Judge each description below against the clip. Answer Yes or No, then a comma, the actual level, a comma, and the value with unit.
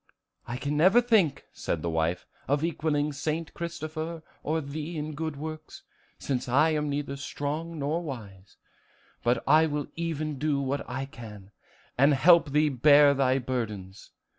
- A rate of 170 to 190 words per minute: No, average, 155 wpm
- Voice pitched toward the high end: No, medium, 145 Hz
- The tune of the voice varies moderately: Yes, average, 3.1 semitones